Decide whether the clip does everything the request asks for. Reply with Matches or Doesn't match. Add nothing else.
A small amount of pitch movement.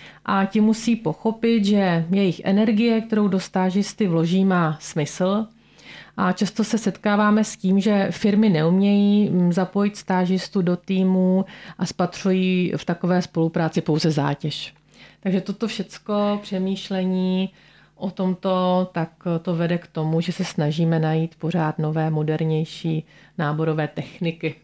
Doesn't match